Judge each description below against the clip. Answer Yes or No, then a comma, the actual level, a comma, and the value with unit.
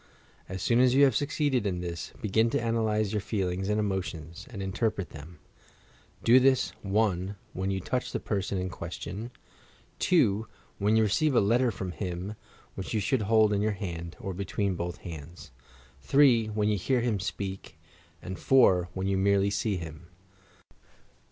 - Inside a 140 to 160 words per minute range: No, average, 170 wpm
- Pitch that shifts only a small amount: No, average, 3.2 semitones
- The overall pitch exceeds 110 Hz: No, low, 100 Hz